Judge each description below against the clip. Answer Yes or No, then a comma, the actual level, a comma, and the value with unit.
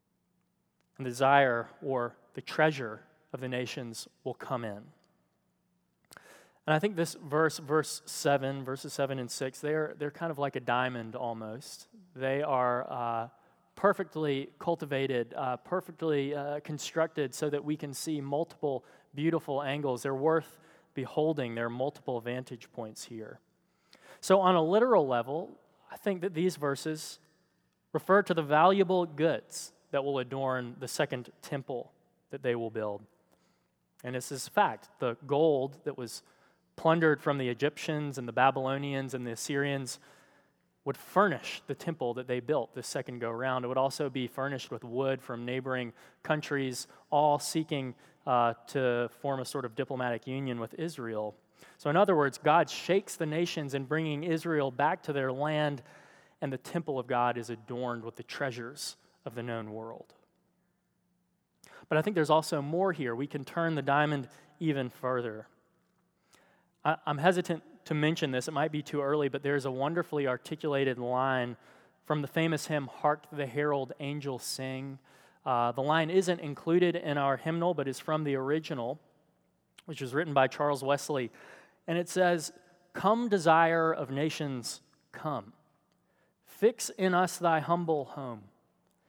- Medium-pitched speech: Yes, medium, 145 Hz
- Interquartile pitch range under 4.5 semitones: Yes, average, 3.6 semitones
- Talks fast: No, average, 155 wpm